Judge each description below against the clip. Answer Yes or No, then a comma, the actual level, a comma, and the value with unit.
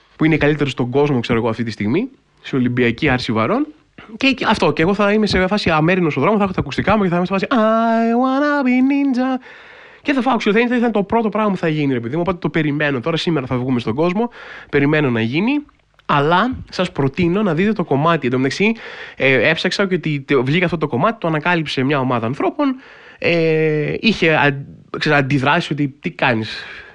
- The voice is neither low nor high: Yes, medium, 170 Hz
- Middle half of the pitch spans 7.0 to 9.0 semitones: Yes, wide, 7.4 semitones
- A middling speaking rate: No, fast, 210 wpm